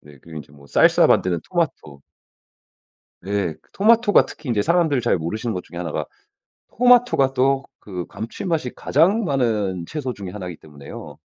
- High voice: No, low, 115 Hz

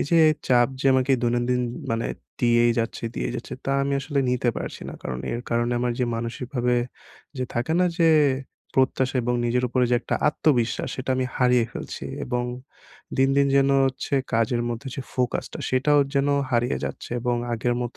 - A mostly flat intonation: Yes, narrow, 1.9 semitones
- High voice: No, low, 125 Hz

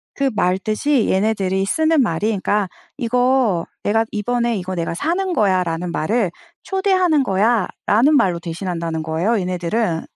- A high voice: Yes, high, 210 Hz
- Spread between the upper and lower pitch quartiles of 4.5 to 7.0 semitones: Yes, wide, 5.6 semitones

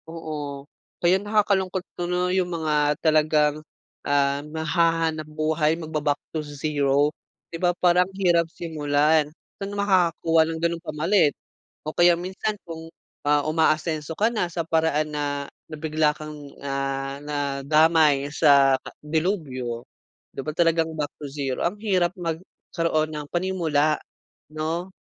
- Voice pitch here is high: No, medium, 155 Hz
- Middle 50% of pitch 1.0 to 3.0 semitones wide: Yes, narrow, 2.6 semitones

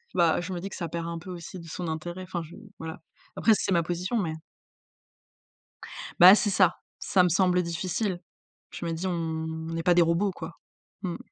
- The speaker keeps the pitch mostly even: Yes, narrow, 1.9 semitones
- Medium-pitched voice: Yes, medium, 175 Hz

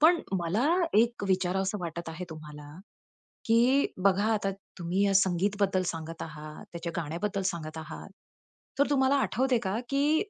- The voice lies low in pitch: No, high, 190 Hz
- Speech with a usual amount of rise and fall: No, wide, 5.9 semitones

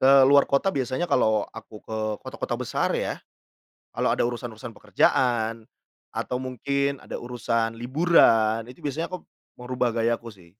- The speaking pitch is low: Yes, low, 120 Hz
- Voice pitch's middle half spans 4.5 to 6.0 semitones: No, average, 3.2 semitones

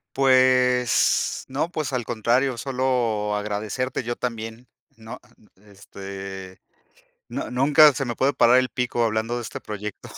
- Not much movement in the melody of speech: No, average, 3.3 semitones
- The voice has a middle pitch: No, low, 120 Hz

